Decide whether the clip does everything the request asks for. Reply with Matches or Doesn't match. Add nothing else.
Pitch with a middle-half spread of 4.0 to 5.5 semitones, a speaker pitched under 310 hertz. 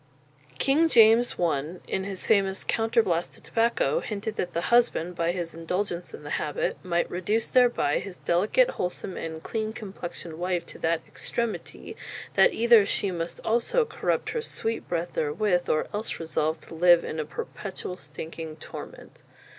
Matches